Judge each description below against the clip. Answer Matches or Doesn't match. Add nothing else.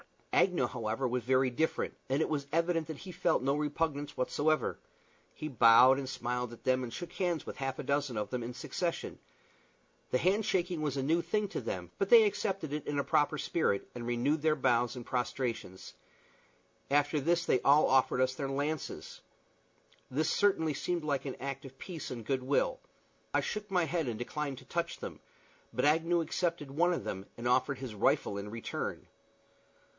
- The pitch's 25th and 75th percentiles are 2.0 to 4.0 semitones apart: Doesn't match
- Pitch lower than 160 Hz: Matches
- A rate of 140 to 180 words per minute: Doesn't match